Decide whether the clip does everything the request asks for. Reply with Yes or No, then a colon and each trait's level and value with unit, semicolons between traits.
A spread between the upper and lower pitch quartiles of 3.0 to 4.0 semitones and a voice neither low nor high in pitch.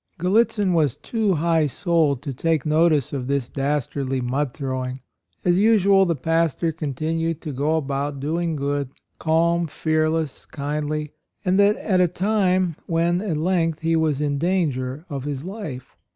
Yes: average, 3.4 semitones; medium, 160 Hz